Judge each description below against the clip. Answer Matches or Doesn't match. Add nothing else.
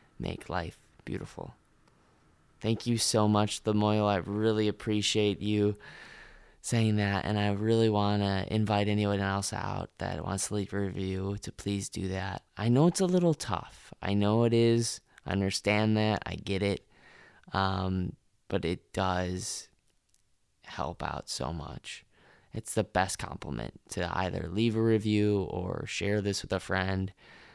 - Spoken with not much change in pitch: Matches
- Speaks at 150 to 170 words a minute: Matches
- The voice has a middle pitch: Doesn't match